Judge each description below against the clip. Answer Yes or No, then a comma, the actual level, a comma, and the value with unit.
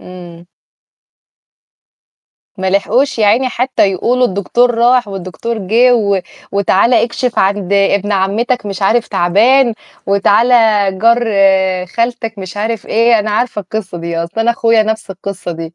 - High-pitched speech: Yes, high, 210 Hz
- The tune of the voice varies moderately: Yes, average, 3.5 semitones